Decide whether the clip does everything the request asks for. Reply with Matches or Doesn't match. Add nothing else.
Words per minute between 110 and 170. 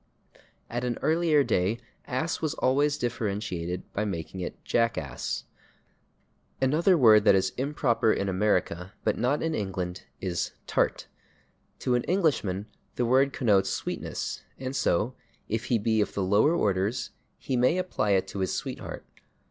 Matches